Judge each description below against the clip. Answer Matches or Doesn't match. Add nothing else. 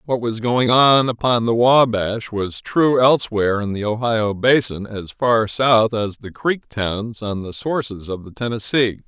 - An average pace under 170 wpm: Doesn't match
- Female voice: Doesn't match